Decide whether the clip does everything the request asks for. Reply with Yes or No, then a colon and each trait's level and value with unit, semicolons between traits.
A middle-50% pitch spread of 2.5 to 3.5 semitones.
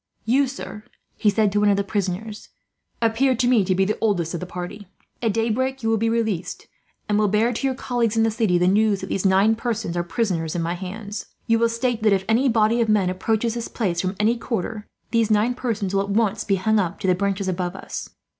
Yes: average, 3.0 semitones